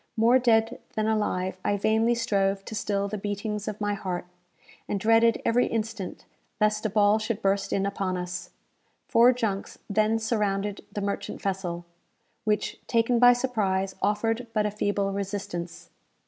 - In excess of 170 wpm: No, average, 155 wpm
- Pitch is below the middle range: No, high, 210 Hz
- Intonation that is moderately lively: No, narrow, 2.3 semitones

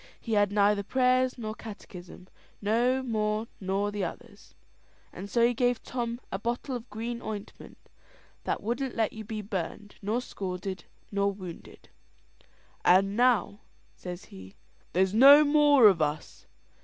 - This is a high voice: Yes, high, 210 Hz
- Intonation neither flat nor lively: Yes, average, 3.5 semitones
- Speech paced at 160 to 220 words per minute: No, average, 145 wpm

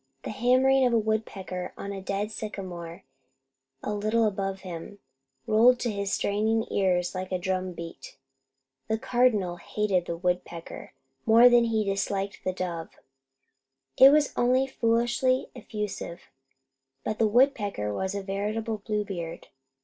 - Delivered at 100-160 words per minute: Yes, slow, 135 wpm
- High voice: Yes, high, 205 Hz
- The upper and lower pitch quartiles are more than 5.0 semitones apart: No, average, 3.6 semitones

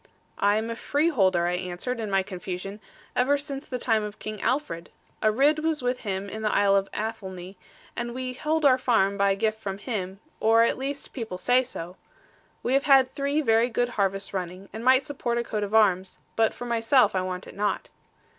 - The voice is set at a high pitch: Yes, high, 220 Hz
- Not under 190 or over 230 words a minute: Yes, fast, 205 wpm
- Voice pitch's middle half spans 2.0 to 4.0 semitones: No, average, 4.6 semitones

